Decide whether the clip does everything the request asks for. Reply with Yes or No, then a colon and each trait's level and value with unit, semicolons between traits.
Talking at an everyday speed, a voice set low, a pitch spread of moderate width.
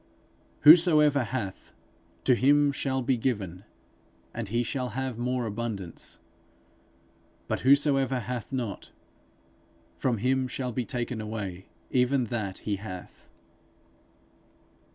No: slow, 110 wpm; low, 125 Hz; average, 3.5 semitones